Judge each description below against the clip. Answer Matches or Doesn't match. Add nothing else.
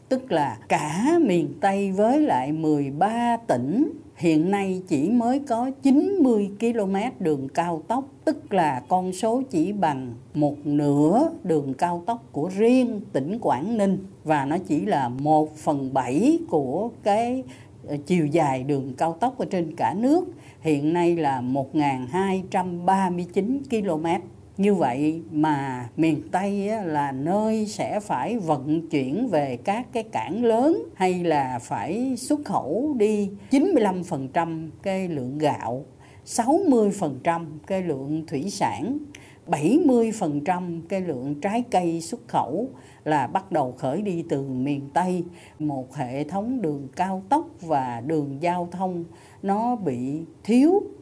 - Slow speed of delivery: Matches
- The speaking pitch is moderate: Matches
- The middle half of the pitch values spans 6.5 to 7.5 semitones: Matches